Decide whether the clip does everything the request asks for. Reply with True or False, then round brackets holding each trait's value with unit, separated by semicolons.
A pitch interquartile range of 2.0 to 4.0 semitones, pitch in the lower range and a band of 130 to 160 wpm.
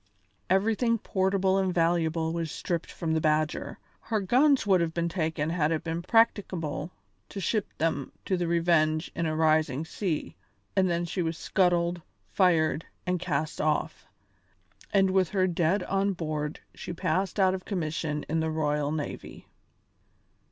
False (3.1 semitones; 170 Hz; 155 wpm)